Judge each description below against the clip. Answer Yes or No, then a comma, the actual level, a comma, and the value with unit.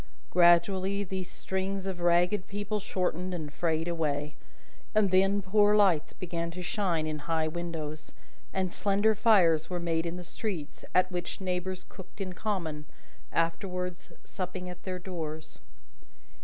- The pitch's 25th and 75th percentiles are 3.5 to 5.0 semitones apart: No, narrow, 2.4 semitones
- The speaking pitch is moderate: Yes, medium, 180 Hz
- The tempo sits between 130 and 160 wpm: Yes, average, 140 wpm